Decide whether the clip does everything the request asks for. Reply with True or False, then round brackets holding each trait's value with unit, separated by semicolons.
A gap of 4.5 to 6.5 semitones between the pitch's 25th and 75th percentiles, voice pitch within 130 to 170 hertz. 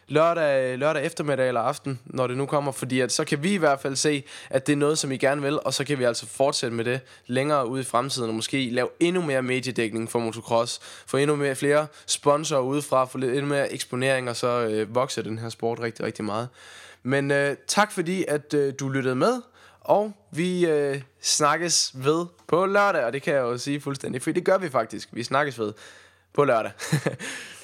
False (3.2 semitones; 135 Hz)